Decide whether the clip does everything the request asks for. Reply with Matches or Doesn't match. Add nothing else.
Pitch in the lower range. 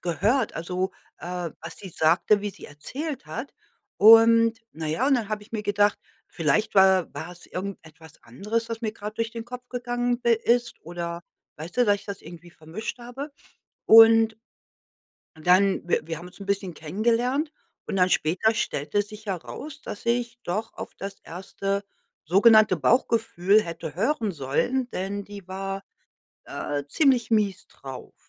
Doesn't match